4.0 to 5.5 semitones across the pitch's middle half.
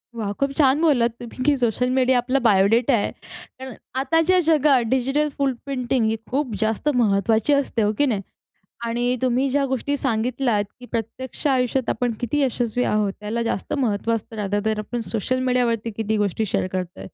No: average, 3.3 semitones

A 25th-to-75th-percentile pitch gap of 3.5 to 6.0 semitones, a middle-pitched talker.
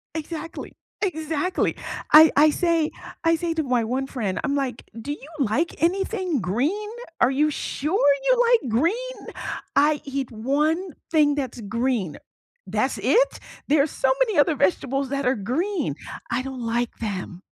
No: average, 4.8 semitones; very high, 285 Hz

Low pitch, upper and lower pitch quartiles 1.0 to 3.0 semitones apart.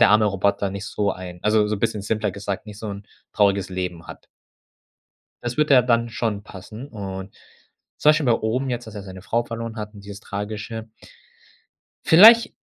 Yes: low, 105 Hz; narrow, 2.6 semitones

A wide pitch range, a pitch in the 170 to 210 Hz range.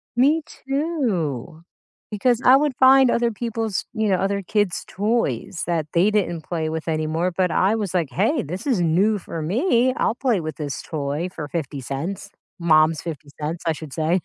Yes: wide, 6.3 semitones; medium, 185 Hz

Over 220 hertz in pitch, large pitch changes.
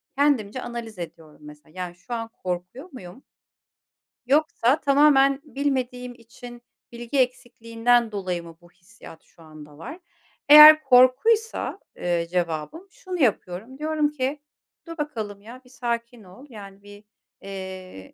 Yes: high, 235 Hz; wide, 6.7 semitones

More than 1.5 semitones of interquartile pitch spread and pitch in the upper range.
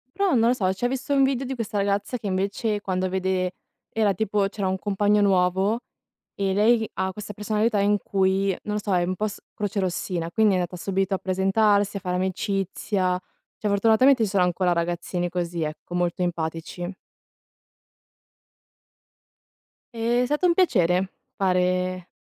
Yes: average, 2.7 semitones; high, 195 Hz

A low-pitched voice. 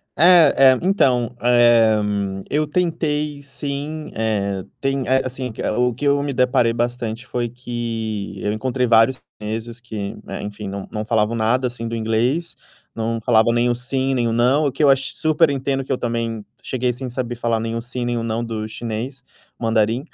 Yes: low, 120 Hz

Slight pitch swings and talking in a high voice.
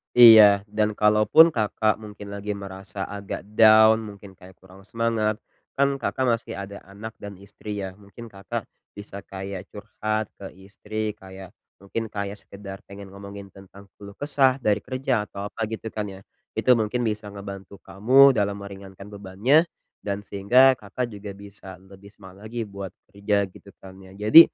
No: narrow, 1.8 semitones; low, 100 Hz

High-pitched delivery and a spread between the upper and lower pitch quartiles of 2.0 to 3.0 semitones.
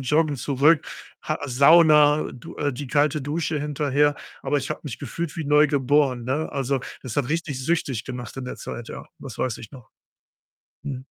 No: medium, 145 Hz; narrow, 2.6 semitones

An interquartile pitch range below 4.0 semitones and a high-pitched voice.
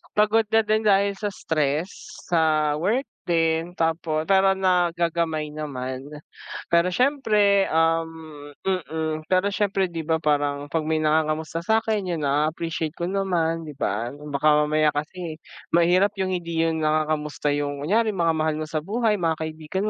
No: average, 3.6 semitones; medium, 165 Hz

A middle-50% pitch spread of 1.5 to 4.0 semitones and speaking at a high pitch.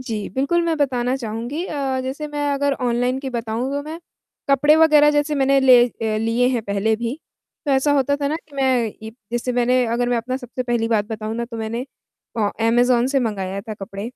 Yes: average, 3.5 semitones; high, 245 Hz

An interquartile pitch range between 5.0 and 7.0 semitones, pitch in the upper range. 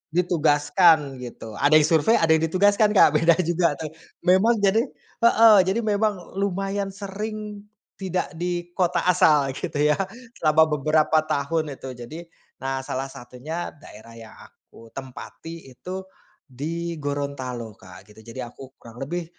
No: wide, 5.5 semitones; medium, 160 Hz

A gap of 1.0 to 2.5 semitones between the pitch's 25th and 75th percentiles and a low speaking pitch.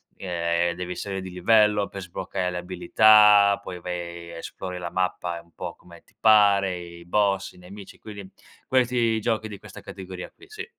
No: average, 2.9 semitones; very low, 95 Hz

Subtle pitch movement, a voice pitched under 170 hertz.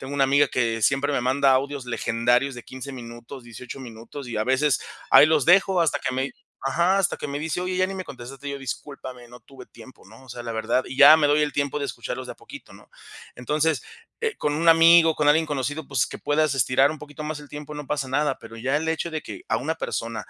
No: average, 3.1 semitones; medium, 140 Hz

